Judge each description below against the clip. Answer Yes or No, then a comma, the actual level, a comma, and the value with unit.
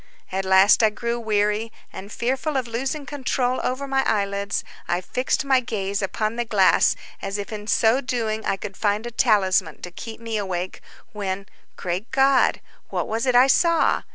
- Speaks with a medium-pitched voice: No, high, 220 Hz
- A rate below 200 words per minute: Yes, average, 180 wpm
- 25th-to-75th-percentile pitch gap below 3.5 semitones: No, average, 3.9 semitones